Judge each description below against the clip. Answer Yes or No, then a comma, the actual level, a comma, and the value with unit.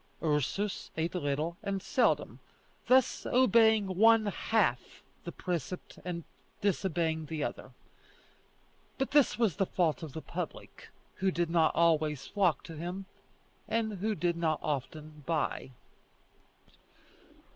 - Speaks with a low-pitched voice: No, medium, 175 Hz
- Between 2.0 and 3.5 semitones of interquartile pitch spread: No, average, 4.3 semitones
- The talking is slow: Yes, slow, 125 wpm